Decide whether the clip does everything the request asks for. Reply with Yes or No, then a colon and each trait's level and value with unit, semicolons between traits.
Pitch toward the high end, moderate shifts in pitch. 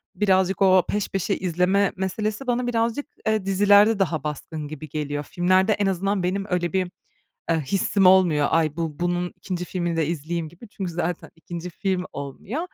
No: medium, 180 Hz; average, 3.1 semitones